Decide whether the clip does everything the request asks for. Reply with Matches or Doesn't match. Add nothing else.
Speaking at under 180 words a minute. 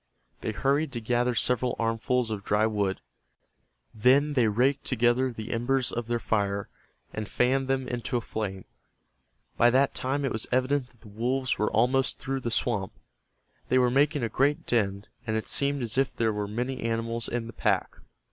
Doesn't match